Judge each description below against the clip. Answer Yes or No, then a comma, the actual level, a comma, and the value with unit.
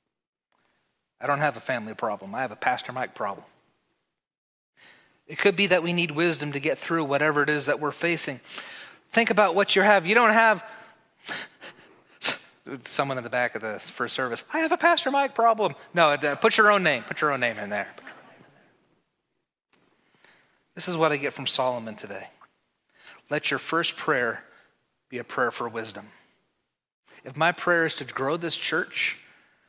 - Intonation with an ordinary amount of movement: No, wide, 6.8 semitones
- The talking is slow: No, average, 180 wpm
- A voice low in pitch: No, medium, 165 Hz